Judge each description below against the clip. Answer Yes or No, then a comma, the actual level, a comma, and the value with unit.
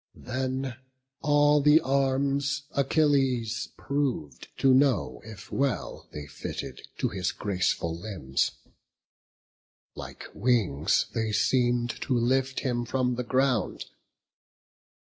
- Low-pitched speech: Yes, low, 130 Hz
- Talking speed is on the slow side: Yes, slow, 105 wpm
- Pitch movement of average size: Yes, average, 3.9 semitones